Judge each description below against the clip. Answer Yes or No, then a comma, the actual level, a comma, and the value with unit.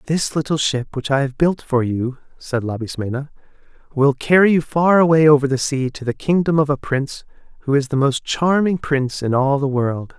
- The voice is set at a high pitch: No, medium, 140 Hz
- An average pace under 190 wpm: No, fast, 205 wpm